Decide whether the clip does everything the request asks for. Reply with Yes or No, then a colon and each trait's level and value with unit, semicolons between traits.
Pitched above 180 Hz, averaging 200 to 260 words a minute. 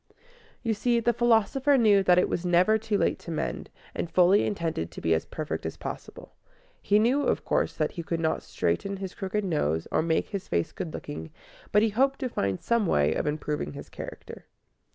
Yes: high, 190 Hz; fast, 205 wpm